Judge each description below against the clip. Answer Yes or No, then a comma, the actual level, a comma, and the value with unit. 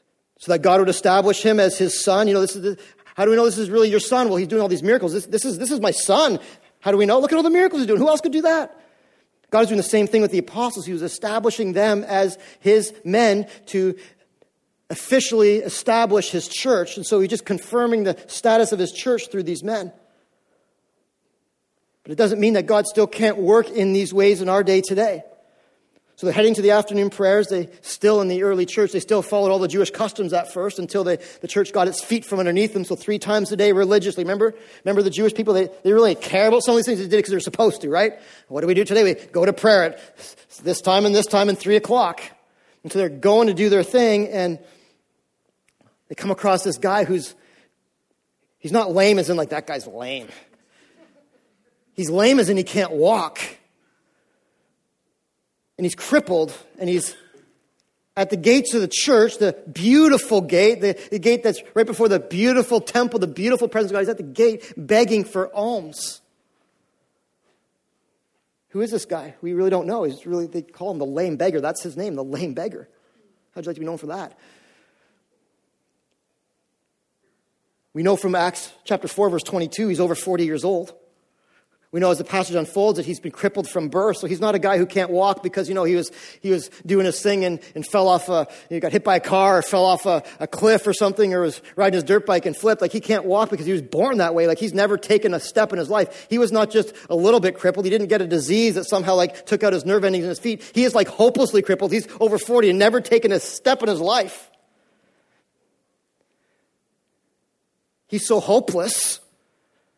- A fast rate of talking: Yes, fast, 220 wpm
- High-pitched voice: Yes, high, 200 Hz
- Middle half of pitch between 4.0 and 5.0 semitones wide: No, average, 3.1 semitones